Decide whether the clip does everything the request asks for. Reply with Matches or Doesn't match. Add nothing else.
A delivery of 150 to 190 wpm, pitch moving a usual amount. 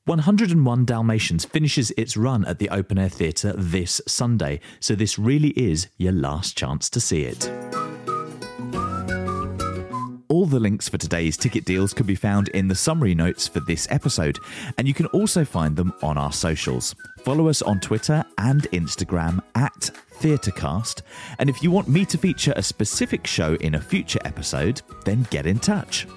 Doesn't match